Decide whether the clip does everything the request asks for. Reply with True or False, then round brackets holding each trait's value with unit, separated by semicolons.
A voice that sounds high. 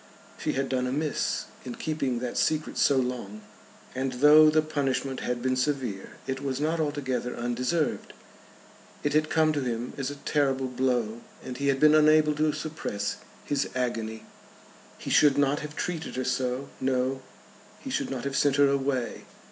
False (135 Hz)